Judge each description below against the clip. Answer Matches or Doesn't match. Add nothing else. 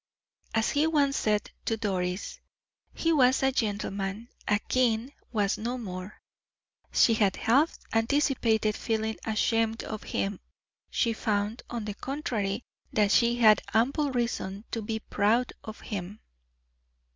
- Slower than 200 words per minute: Matches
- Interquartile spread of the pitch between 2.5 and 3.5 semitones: Matches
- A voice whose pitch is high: Matches